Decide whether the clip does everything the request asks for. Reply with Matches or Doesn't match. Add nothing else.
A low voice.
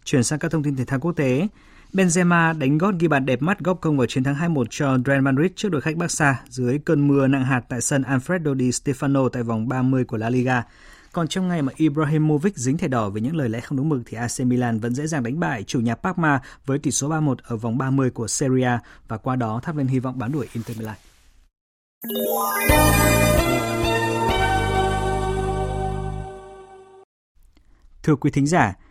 Matches